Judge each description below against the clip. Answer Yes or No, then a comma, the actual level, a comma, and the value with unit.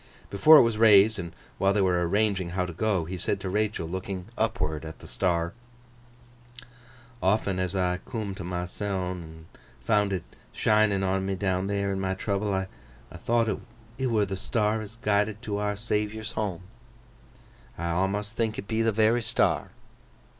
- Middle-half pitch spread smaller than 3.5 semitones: Yes, average, 2.7 semitones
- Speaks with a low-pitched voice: Yes, low, 100 Hz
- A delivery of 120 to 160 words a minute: No, average, 170 wpm